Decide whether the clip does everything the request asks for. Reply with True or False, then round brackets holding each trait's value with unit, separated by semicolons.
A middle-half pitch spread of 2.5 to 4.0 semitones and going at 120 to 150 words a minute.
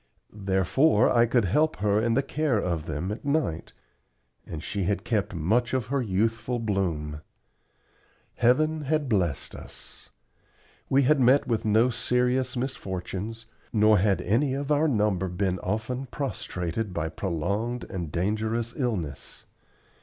False (5.0 semitones; 140 wpm)